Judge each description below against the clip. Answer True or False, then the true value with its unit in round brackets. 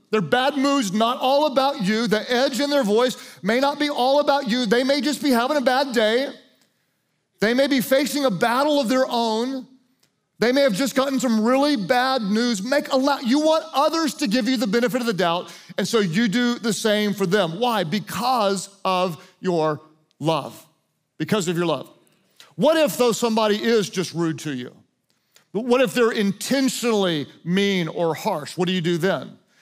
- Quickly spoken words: False (195 wpm)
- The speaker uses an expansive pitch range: True (5.7 semitones)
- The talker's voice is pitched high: True (235 Hz)